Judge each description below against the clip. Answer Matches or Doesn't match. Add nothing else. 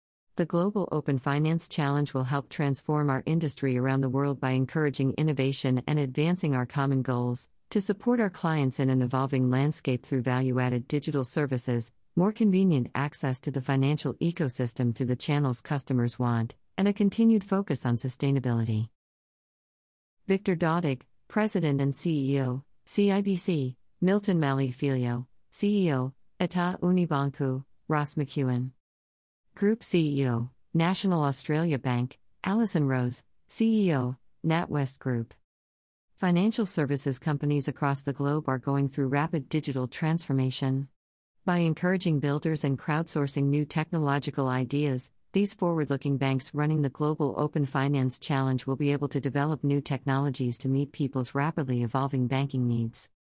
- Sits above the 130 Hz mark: Matches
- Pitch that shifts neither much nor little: Matches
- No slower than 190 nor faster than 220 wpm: Doesn't match